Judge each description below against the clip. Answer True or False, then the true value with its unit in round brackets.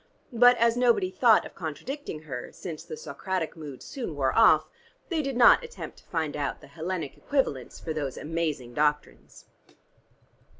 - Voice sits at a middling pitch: True (165 Hz)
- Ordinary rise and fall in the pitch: False (8.1 semitones)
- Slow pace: False (160 wpm)